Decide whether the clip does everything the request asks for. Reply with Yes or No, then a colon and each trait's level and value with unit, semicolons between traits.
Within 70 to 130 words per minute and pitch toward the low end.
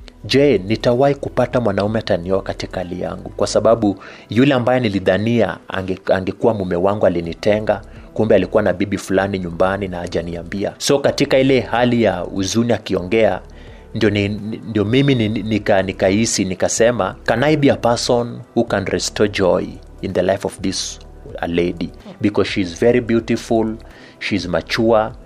No: fast, 140 wpm; low, 100 Hz